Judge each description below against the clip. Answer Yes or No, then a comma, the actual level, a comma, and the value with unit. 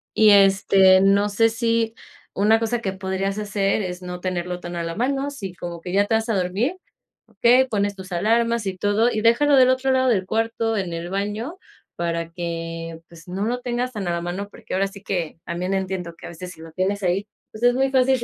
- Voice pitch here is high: Yes, high, 200 Hz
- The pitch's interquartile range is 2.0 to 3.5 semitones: No, average, 4.1 semitones